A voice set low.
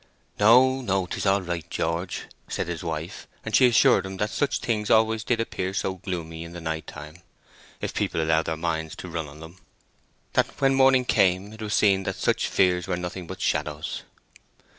Yes: very low, 90 Hz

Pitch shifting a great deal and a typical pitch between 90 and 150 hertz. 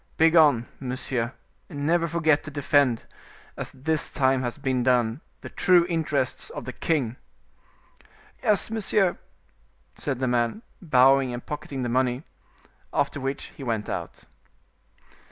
No: average, 4.1 semitones; low, 135 Hz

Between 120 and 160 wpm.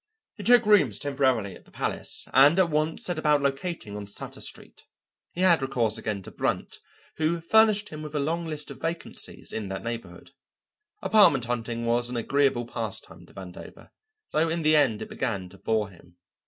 No: average, 185 wpm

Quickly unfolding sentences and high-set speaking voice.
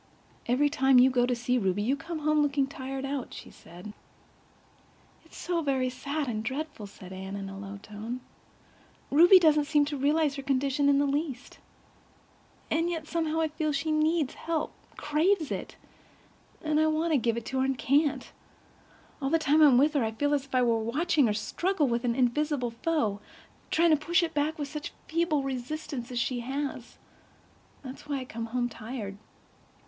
No: average, 185 wpm; very high, 275 Hz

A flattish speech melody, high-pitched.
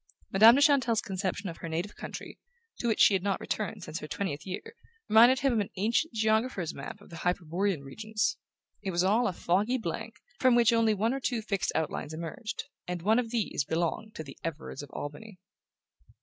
No: average, 4.9 semitones; high, 205 Hz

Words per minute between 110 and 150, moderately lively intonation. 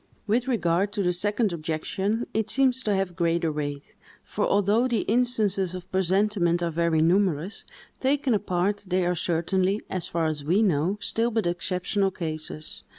No: average, 160 wpm; average, 3.8 semitones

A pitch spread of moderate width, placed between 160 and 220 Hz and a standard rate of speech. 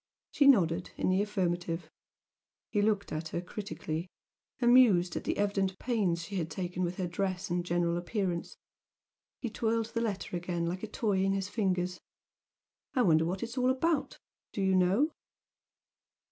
Yes: average, 3.7 semitones; high, 190 Hz; average, 160 wpm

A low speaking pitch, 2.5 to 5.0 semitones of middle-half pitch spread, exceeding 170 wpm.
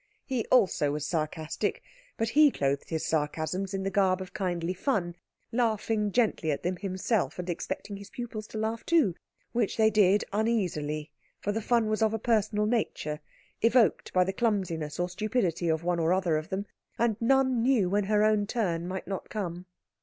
No: high, 195 Hz; average, 4.2 semitones; average, 185 wpm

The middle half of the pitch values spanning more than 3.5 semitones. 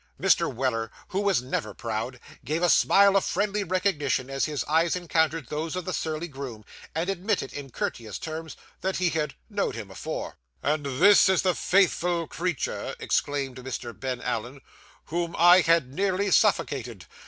Yes: wide, 5.4 semitones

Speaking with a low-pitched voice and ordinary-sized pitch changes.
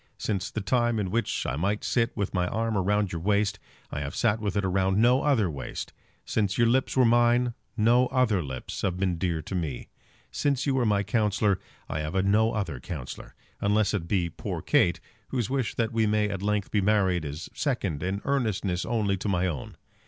Yes: low, 105 Hz; average, 3.8 semitones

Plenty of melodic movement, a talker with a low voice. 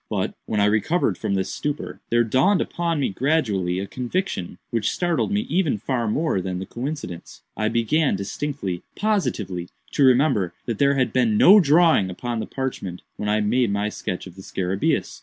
Yes: wide, 7.1 semitones; low, 120 Hz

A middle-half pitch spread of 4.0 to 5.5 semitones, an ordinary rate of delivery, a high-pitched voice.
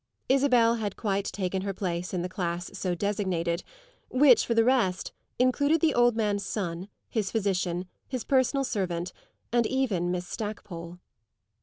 Yes: average, 5.1 semitones; average, 150 wpm; high, 200 Hz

